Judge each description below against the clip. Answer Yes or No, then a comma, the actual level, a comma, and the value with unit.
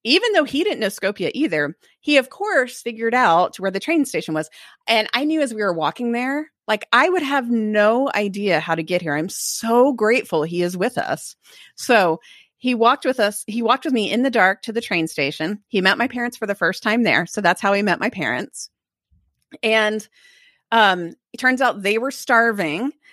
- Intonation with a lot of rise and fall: No, average, 4.7 semitones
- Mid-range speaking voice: No, high, 225 Hz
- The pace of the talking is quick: Yes, fast, 215 wpm